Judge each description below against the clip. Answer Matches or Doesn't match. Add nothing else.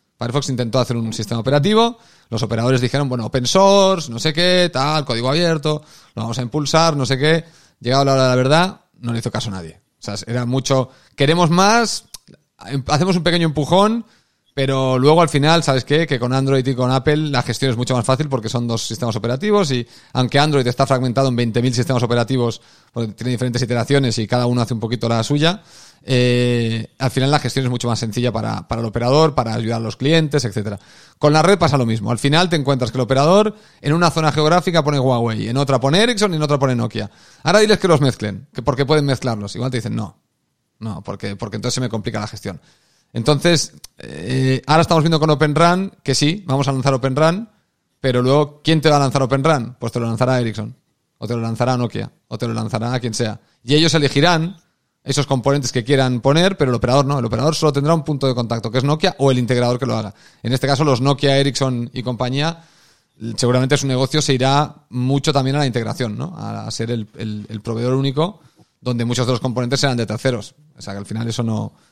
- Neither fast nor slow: Doesn't match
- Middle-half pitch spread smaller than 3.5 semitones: Doesn't match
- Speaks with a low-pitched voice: Matches